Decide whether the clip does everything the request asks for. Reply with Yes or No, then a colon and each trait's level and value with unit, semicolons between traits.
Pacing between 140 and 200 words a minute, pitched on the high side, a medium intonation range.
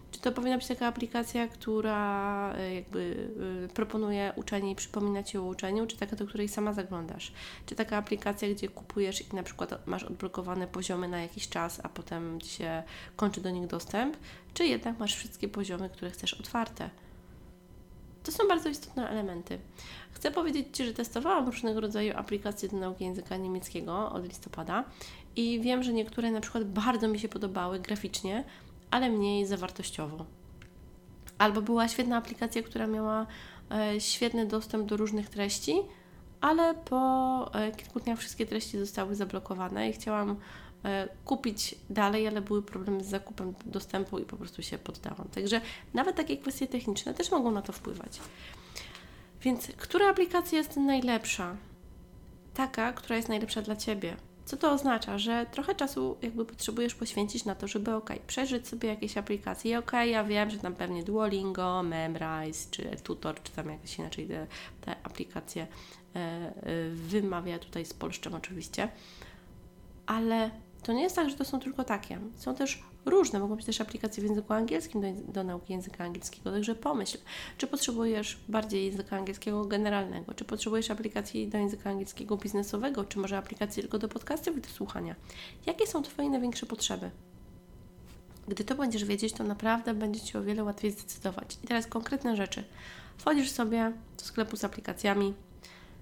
Yes: fast, 160 wpm; high, 215 Hz; average, 3.0 semitones